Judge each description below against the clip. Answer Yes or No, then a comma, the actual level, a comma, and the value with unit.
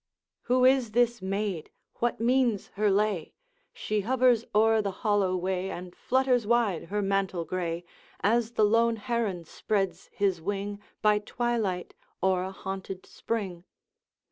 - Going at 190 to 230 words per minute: No, average, 140 wpm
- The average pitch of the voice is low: No, high, 205 Hz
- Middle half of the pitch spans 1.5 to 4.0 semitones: Yes, average, 3.6 semitones